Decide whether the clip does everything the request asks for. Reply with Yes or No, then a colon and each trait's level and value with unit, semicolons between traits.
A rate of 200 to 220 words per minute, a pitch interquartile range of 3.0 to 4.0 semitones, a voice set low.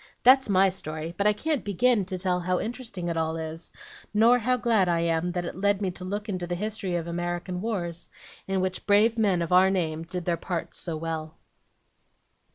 No: fast, 205 wpm; average, 3.3 semitones; medium, 185 Hz